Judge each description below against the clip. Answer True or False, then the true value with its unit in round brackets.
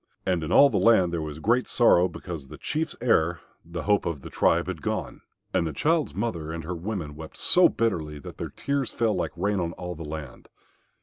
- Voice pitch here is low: True (90 Hz)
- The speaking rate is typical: False (220 wpm)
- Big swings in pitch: True (6.1 semitones)